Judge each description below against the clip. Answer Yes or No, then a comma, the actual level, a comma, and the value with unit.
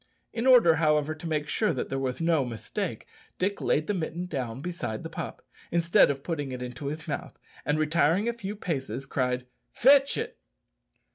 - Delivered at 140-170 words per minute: No, average, 185 wpm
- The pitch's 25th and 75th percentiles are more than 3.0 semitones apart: Yes, average, 4.7 semitones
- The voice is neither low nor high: Yes, medium, 155 Hz